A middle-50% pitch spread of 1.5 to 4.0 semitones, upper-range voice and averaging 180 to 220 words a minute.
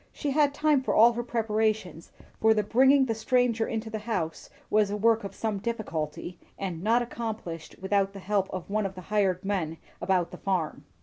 Yes: average, 3.4 semitones; high, 210 Hz; average, 195 wpm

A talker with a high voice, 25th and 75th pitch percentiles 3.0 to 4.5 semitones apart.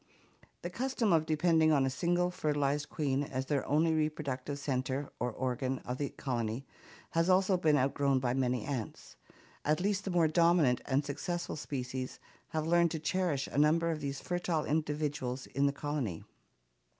No: medium, 145 Hz; average, 3.8 semitones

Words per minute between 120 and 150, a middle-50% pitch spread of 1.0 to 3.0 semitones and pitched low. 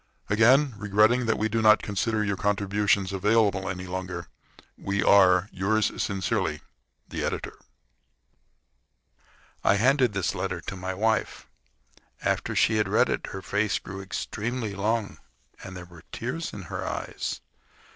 Yes: average, 140 wpm; narrow, 2.5 semitones; low, 100 Hz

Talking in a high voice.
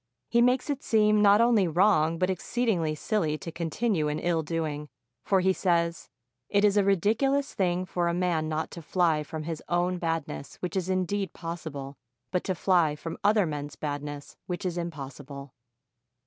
No: medium, 175 Hz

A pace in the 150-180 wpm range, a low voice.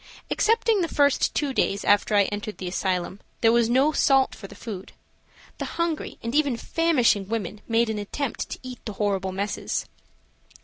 No: average, 175 wpm; high, 230 Hz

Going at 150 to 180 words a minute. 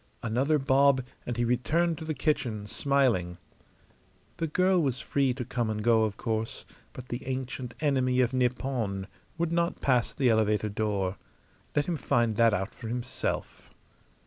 Yes: average, 160 wpm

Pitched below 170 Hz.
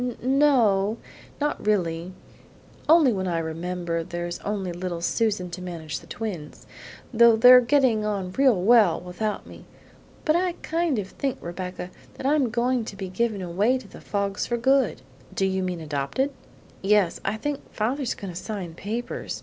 No: high, 205 Hz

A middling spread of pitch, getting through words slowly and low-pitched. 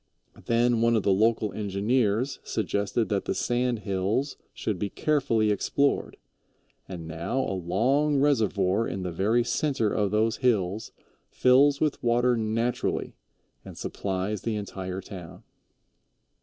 Yes: average, 4.0 semitones; slow, 130 wpm; low, 110 Hz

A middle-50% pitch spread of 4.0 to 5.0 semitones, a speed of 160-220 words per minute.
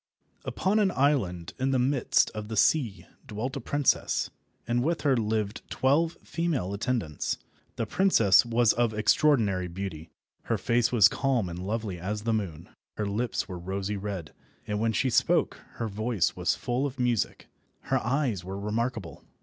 Yes: average, 4.6 semitones; average, 165 wpm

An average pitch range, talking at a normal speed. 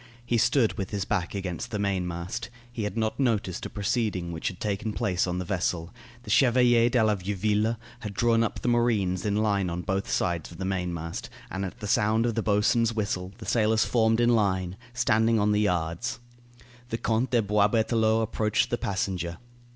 Yes: average, 3.3 semitones; average, 190 wpm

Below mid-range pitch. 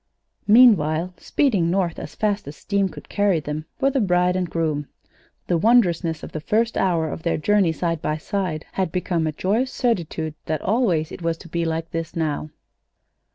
No: medium, 170 Hz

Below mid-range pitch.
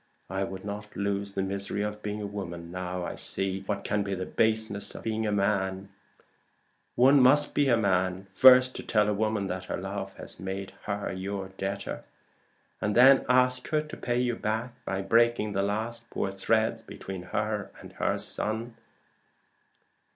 Yes: low, 105 Hz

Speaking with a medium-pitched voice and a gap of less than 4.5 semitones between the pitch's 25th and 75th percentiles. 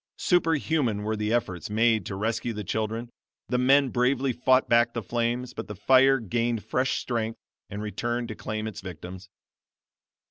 No: low, 115 Hz; average, 2.8 semitones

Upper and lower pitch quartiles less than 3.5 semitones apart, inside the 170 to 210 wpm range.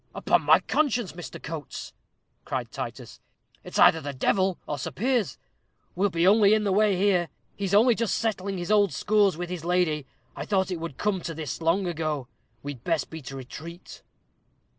No: average, 4.0 semitones; average, 185 wpm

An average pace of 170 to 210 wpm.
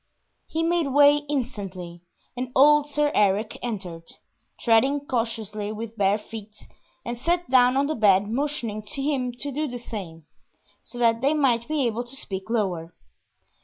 No: average, 155 wpm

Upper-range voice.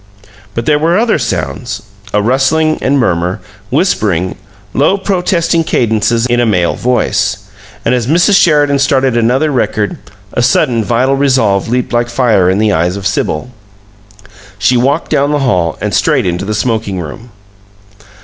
No: low, 120 Hz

